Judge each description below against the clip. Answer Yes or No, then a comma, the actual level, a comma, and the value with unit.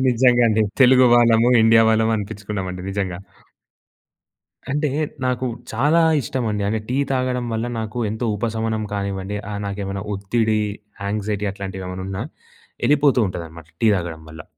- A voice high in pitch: No, low, 110 Hz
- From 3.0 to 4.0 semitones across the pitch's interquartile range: Yes, average, 3.6 semitones